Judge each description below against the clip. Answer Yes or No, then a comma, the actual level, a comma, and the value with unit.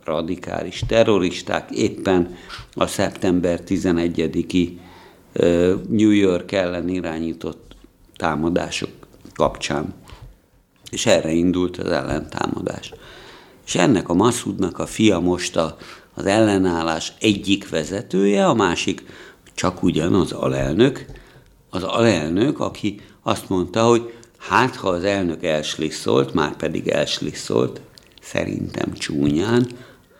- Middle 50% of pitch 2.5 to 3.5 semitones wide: Yes, average, 2.9 semitones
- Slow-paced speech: Yes, slow, 100 wpm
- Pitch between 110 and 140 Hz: No, very low, 90 Hz